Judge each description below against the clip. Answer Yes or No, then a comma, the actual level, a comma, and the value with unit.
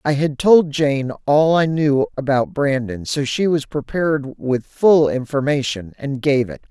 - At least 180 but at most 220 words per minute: No, average, 170 wpm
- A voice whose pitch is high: No, medium, 140 Hz